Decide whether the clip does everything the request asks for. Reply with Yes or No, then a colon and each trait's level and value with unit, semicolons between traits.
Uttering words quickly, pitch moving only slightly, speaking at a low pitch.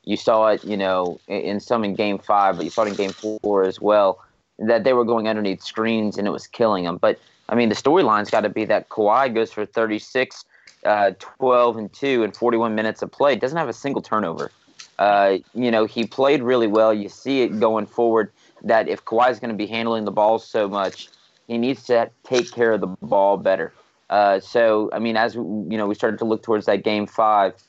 Yes: fast, 230 wpm; narrow, 2.3 semitones; low, 110 Hz